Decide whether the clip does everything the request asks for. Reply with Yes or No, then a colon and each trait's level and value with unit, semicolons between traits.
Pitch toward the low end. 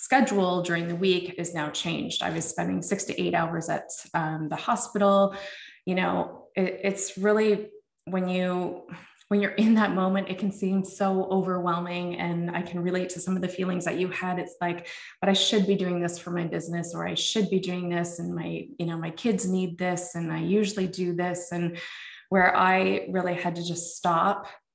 No: medium, 180 Hz